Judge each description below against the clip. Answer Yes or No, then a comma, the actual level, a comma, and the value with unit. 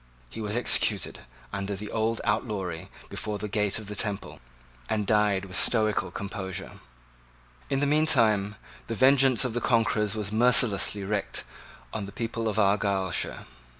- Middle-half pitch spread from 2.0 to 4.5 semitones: Yes, narrow, 2.4 semitones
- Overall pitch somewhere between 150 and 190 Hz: No, low, 105 Hz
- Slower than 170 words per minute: Yes, average, 150 wpm